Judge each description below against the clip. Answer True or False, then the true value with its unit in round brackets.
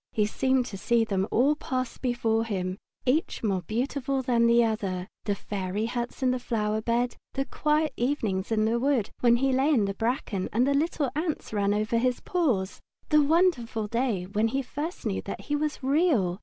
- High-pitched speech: True (235 Hz)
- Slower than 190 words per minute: False (195 wpm)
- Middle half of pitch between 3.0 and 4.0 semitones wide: False (4.4 semitones)